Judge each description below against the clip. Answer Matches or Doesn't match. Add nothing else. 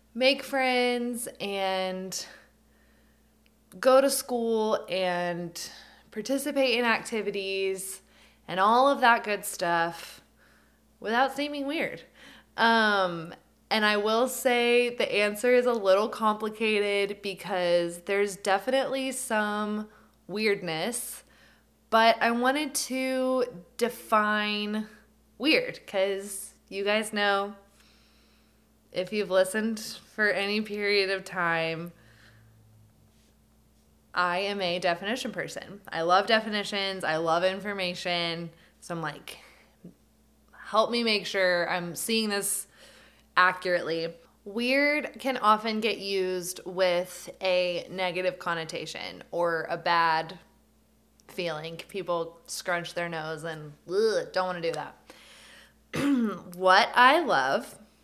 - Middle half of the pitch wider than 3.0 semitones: Matches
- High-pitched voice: Matches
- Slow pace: Matches